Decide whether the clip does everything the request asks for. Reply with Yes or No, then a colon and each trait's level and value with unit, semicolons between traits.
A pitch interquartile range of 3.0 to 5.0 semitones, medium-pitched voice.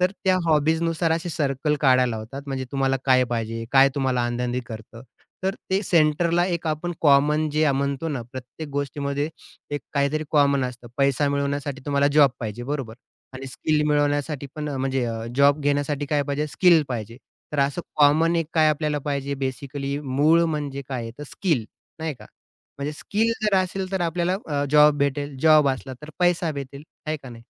No: narrow, 2.6 semitones; medium, 145 Hz